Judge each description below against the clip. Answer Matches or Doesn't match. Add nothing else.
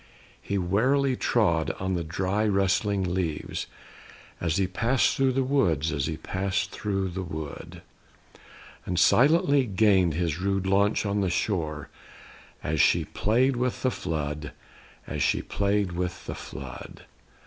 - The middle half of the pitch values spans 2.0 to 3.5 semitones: Doesn't match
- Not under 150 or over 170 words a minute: Doesn't match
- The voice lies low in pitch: Matches